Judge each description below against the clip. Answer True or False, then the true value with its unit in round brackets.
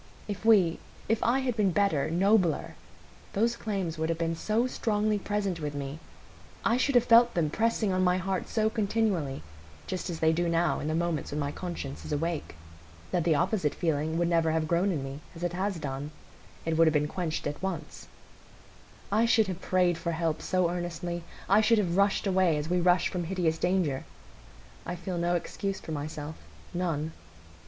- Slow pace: False (185 wpm)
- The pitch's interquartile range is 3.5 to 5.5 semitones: True (3.8 semitones)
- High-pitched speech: False (175 Hz)